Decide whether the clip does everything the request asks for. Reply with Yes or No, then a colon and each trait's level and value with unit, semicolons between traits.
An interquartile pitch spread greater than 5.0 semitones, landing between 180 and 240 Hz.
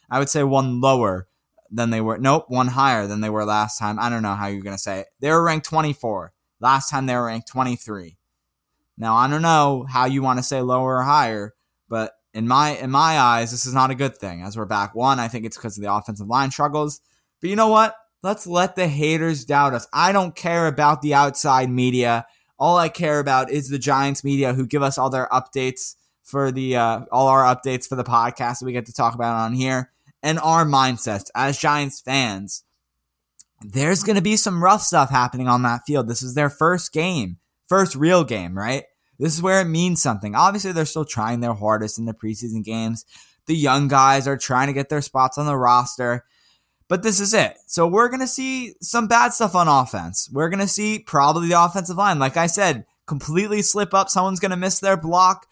No: wide, 5.5 semitones; low, 135 Hz